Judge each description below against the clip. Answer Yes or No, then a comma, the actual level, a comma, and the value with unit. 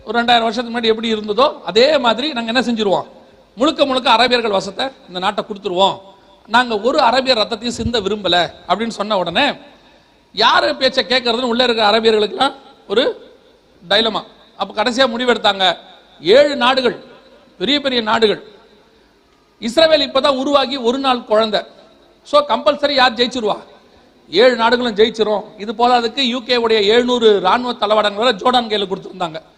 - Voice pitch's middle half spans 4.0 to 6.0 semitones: No, average, 3.4 semitones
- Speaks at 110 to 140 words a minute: Yes, fast, 130 wpm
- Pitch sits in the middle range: No, high, 235 Hz